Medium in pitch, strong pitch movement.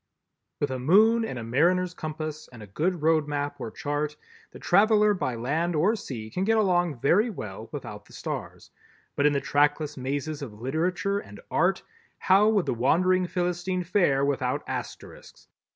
No: medium, 155 Hz; average, 4.7 semitones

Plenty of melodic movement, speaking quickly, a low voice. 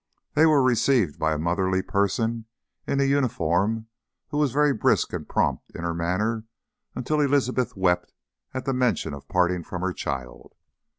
No: wide, 6.7 semitones; average, 165 wpm; low, 110 Hz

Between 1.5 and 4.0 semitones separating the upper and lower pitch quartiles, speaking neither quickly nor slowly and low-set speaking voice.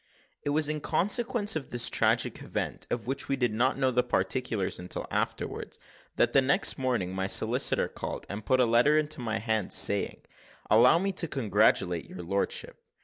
No: average, 5.1 semitones; average, 180 wpm; low, 125 Hz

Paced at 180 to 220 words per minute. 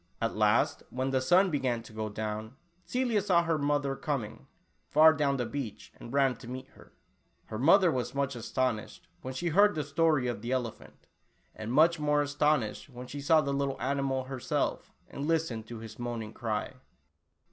Yes: average, 185 wpm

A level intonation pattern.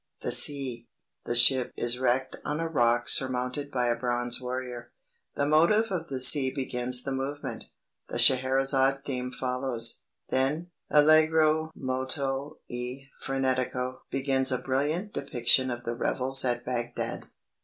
Yes: narrow, 2.2 semitones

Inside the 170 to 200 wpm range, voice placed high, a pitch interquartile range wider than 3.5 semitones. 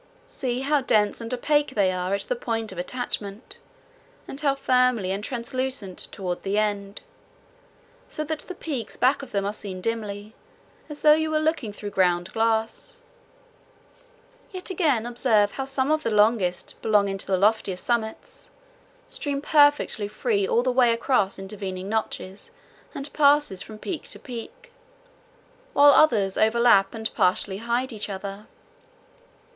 No: average, 150 wpm; high, 225 Hz; wide, 5.5 semitones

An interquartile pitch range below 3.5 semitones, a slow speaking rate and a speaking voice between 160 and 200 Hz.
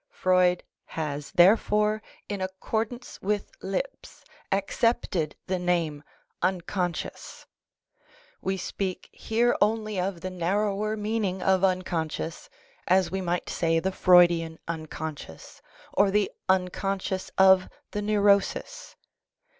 Yes: average, 2.8 semitones; slow, 105 wpm; high, 190 Hz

